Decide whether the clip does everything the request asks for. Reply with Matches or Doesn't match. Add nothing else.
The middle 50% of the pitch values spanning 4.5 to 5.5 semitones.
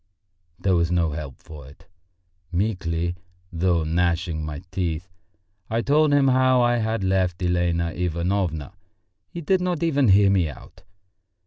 Matches